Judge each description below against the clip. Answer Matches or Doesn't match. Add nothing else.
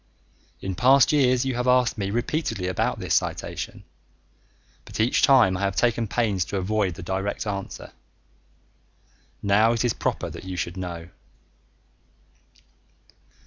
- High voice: Doesn't match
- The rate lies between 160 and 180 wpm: Doesn't match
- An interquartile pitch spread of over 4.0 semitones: Matches